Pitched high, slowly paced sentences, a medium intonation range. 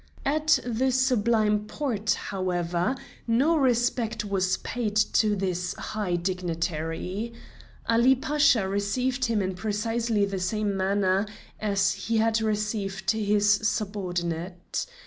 Yes: high, 210 Hz; slow, 110 wpm; average, 3.4 semitones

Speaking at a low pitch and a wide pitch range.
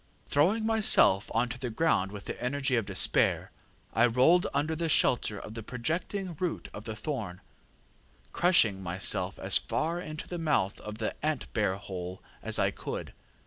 Yes: low, 125 Hz; wide, 7.8 semitones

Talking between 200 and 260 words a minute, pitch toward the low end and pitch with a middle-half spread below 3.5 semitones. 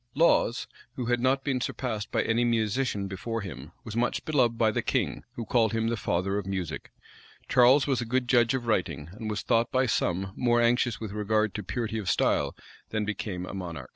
Yes: fast, 205 wpm; low, 115 Hz; average, 3.1 semitones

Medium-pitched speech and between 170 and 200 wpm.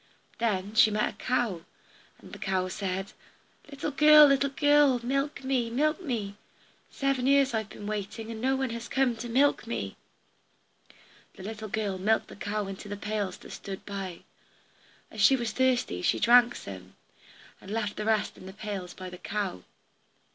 No: high, 220 Hz; average, 175 wpm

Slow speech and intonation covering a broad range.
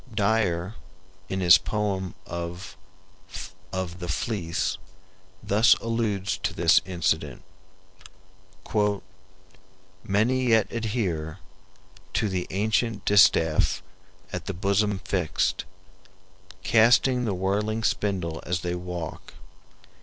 No: slow, 95 wpm; average, 3.5 semitones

